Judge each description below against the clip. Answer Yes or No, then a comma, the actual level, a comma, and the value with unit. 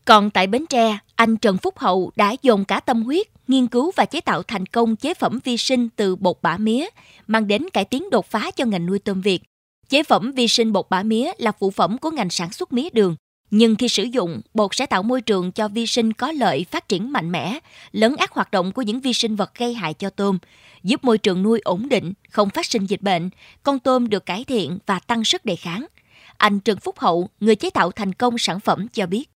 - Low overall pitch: No, high, 220 Hz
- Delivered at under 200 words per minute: No, average, 245 wpm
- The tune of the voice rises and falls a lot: No, average, 3.9 semitones